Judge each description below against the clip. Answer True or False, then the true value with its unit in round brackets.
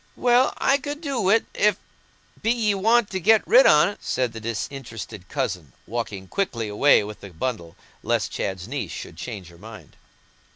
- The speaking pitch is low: True (125 Hz)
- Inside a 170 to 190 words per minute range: True (175 wpm)